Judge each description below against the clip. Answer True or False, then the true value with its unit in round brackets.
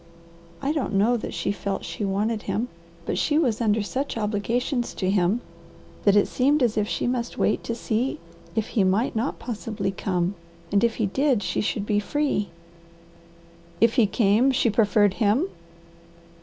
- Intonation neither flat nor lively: True (3.3 semitones)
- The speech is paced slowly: False (170 wpm)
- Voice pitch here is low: False (220 Hz)